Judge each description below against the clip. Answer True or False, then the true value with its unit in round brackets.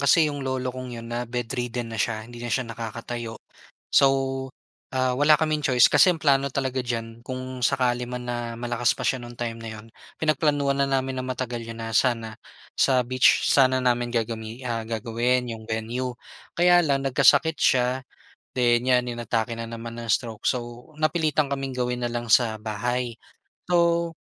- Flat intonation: True (2.2 semitones)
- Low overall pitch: True (125 Hz)